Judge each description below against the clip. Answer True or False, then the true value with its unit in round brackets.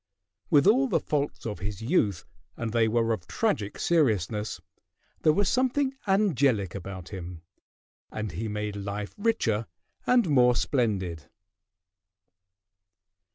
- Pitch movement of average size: False (7.2 semitones)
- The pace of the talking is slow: True (120 wpm)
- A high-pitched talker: False (110 Hz)